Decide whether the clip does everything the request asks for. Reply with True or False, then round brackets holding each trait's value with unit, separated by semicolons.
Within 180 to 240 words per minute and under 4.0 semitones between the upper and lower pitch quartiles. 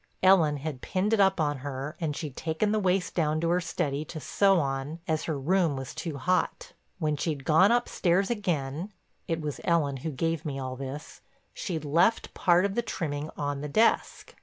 False (185 wpm; 4.3 semitones)